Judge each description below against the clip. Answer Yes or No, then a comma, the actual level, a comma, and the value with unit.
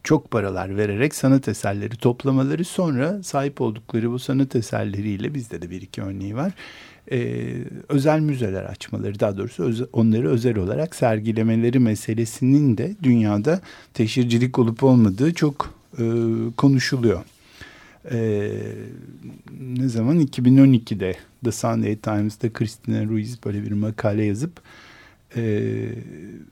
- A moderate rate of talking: Yes, average, 120 wpm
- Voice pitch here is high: No, low, 115 Hz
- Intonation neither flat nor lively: Yes, average, 3.7 semitones